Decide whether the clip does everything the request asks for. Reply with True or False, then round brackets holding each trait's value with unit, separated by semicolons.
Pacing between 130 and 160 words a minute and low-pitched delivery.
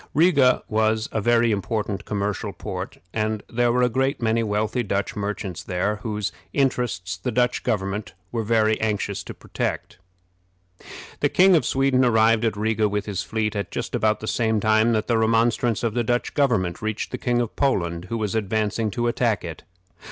False (180 wpm; 110 Hz)